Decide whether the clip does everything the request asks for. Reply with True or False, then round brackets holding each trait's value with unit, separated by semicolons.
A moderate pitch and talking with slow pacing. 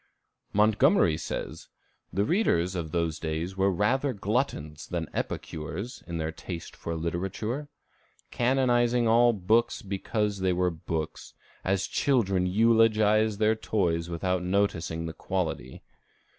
False (95 Hz; 120 wpm)